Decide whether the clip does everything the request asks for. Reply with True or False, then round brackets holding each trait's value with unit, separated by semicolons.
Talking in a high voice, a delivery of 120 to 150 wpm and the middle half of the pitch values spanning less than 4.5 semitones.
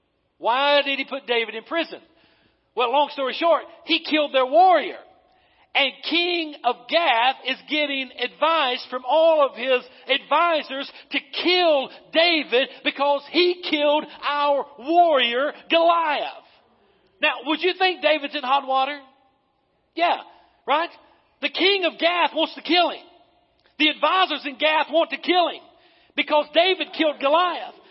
True (300 Hz; 140 wpm; 3.4 semitones)